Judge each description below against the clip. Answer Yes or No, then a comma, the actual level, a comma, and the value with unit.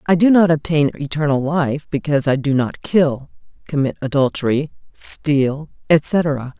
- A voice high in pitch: No, medium, 145 Hz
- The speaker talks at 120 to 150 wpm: Yes, slow, 135 wpm